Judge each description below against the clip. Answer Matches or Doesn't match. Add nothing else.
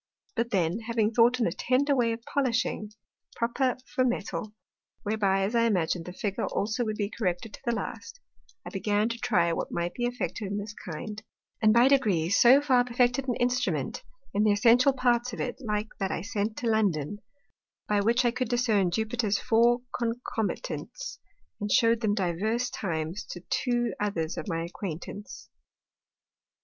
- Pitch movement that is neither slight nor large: Matches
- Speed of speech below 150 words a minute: Doesn't match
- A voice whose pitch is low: Doesn't match